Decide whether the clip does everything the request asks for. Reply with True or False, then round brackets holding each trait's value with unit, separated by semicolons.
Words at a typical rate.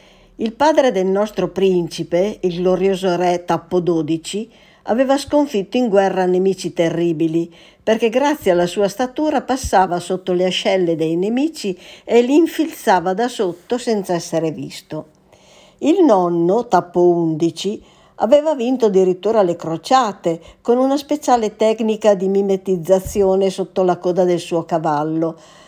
True (130 wpm)